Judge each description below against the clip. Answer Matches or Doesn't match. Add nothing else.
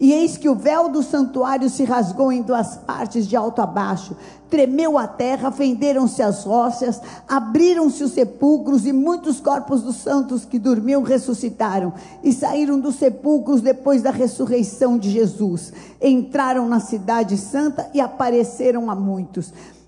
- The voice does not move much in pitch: Doesn't match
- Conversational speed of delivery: Matches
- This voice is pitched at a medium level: Doesn't match